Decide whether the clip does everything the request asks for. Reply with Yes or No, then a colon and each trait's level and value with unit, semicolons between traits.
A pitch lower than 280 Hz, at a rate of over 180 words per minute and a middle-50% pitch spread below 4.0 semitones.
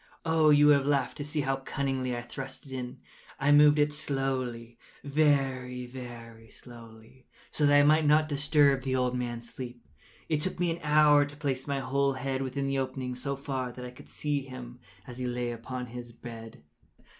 Yes: low, 135 Hz; average, 190 wpm; average, 2.7 semitones